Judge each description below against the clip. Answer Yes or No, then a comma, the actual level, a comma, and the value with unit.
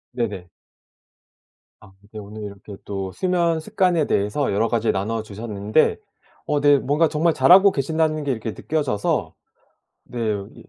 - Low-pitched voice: Yes, low, 120 Hz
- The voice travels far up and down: Yes, wide, 7.1 semitones